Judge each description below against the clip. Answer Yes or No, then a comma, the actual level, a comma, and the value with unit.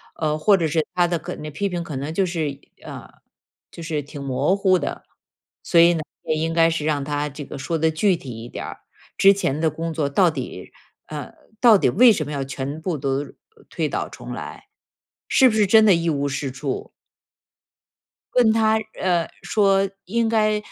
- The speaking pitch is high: No, medium, 165 Hz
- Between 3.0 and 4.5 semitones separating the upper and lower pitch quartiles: No, average, 4.9 semitones